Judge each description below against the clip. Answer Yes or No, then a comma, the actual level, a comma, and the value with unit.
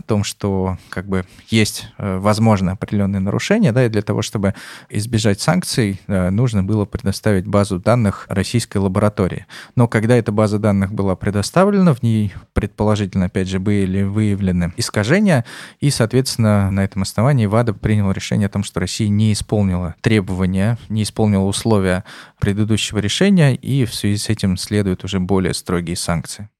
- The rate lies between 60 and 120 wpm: No, average, 155 wpm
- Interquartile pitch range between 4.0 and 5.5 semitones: No, narrow, 2.5 semitones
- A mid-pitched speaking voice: No, low, 105 Hz